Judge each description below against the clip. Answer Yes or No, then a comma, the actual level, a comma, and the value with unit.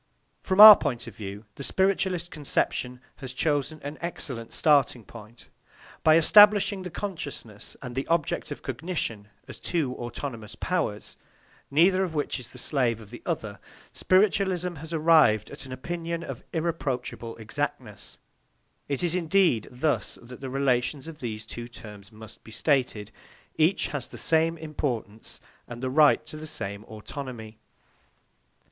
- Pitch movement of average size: No, wide, 5.9 semitones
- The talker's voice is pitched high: No, medium, 140 Hz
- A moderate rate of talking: Yes, average, 150 wpm